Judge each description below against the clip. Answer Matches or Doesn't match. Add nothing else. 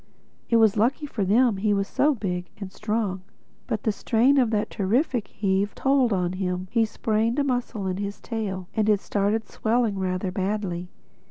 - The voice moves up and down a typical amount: Matches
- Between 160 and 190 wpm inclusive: Matches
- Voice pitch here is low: Doesn't match